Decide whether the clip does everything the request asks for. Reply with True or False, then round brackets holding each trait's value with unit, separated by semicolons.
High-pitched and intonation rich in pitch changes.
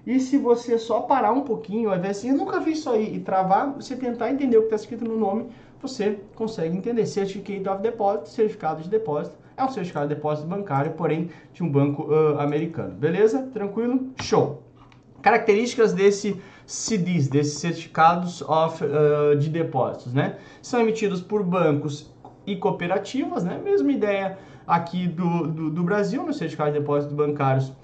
True (195 Hz; 6.1 semitones)